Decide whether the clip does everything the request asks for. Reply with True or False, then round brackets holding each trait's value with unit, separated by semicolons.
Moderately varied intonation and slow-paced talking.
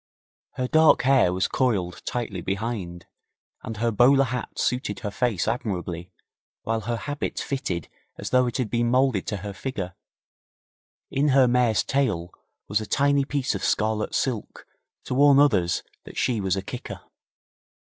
False (5.0 semitones; 155 wpm)